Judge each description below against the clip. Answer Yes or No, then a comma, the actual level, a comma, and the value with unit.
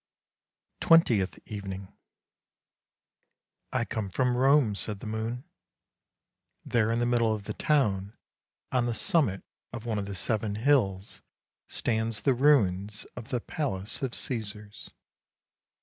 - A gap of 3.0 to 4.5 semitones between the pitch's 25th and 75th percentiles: Yes, average, 3.4 semitones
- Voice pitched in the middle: No, low, 110 Hz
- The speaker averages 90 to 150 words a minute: Yes, slow, 135 wpm